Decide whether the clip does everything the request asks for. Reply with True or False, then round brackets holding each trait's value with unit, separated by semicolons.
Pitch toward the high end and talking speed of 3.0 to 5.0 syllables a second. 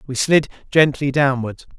False (140 Hz; 4.5 syllables/s)